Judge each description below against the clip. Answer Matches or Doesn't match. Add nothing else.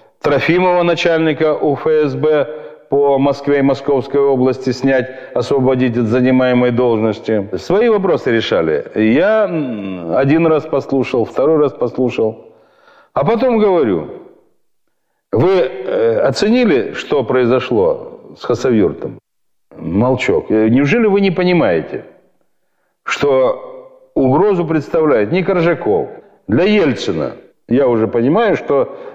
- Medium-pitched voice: Matches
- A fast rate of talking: Doesn't match